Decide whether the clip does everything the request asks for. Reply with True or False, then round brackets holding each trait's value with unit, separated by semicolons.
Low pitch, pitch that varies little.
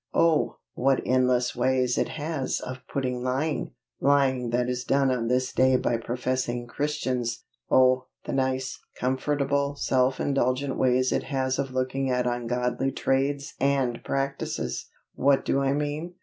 True (130 Hz; 1.6 semitones)